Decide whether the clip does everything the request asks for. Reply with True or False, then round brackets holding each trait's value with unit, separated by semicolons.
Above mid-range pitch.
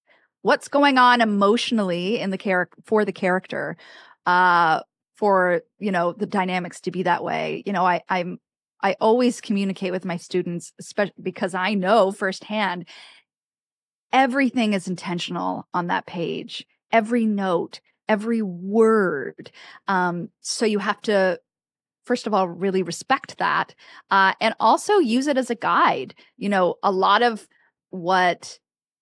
True (195 Hz)